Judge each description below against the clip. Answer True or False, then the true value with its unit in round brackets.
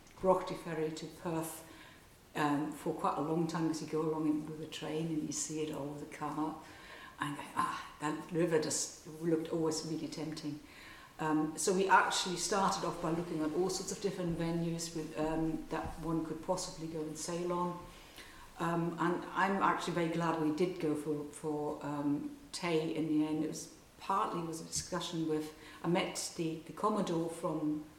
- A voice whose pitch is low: False (160 Hz)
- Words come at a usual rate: True (190 wpm)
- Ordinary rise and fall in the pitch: False (1.9 semitones)